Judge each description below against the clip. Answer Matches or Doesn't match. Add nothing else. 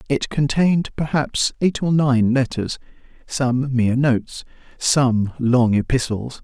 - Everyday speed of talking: Doesn't match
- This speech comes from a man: Matches